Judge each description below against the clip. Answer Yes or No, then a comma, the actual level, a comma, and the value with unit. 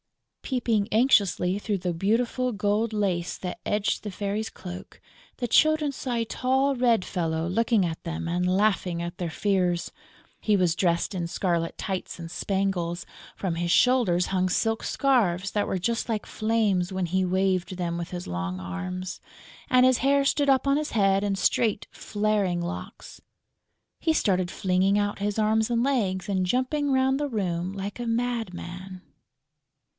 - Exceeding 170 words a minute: No, average, 165 wpm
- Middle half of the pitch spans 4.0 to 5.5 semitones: Yes, average, 4.4 semitones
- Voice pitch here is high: Yes, high, 195 Hz